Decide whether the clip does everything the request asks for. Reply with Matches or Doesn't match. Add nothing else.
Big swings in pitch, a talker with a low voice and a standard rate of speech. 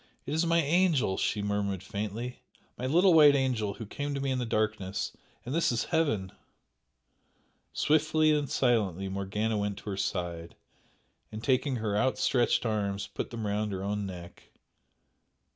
Matches